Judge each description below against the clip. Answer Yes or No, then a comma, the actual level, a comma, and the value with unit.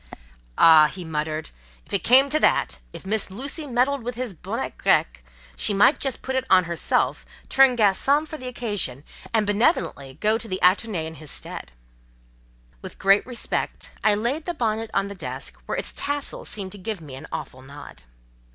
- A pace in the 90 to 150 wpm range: No, average, 180 wpm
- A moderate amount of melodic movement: No, wide, 7.7 semitones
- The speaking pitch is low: No, high, 205 Hz